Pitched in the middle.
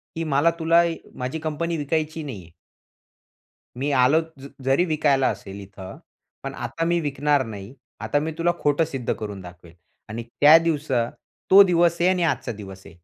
Yes: medium, 145 Hz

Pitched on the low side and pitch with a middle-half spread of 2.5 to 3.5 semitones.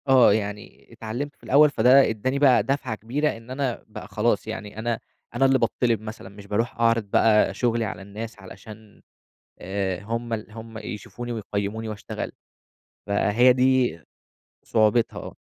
Yes: low, 115 Hz; average, 2.8 semitones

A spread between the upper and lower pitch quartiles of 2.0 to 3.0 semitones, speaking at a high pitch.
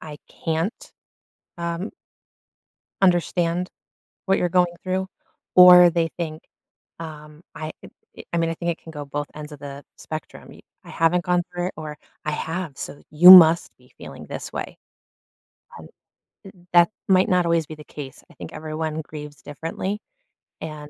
No: narrow, 2.6 semitones; medium, 165 Hz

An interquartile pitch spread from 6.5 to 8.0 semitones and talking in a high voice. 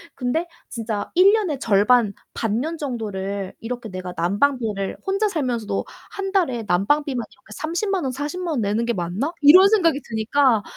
Yes: wide, 7.2 semitones; very high, 250 Hz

